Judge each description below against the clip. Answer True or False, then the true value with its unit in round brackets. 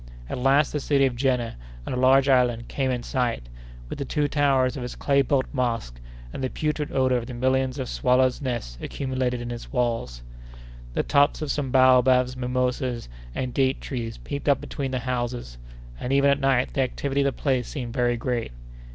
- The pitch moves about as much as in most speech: False (1.8 semitones)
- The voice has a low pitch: True (130 Hz)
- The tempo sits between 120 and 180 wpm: False (195 wpm)